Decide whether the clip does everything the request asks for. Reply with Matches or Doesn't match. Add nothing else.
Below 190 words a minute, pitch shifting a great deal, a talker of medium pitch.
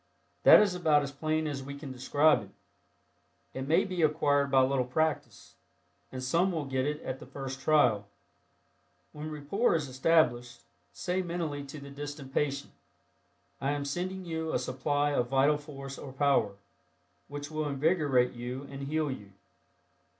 Doesn't match